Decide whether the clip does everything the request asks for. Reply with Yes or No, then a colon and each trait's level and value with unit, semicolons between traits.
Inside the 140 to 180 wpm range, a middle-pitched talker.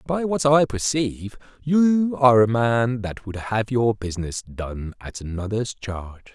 No: average, 160 wpm; low, 120 Hz